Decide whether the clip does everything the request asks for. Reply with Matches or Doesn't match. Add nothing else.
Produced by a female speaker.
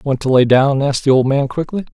Doesn't match